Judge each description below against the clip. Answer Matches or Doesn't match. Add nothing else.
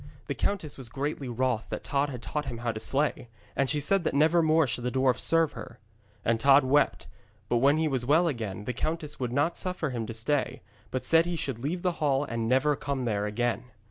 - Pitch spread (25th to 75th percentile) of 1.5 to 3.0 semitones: Doesn't match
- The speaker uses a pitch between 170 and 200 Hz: Doesn't match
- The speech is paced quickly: Matches